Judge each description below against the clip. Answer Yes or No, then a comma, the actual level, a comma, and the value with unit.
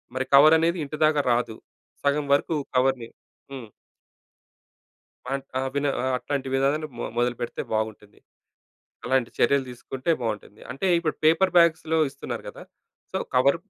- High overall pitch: No, low, 135 Hz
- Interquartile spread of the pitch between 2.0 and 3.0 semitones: No, average, 4.0 semitones